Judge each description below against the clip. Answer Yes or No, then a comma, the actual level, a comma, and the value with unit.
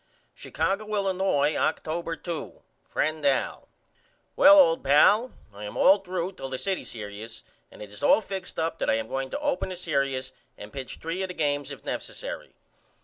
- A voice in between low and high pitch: Yes, medium, 160 Hz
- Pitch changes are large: Yes, wide, 6.2 semitones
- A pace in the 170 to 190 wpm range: Yes, average, 180 wpm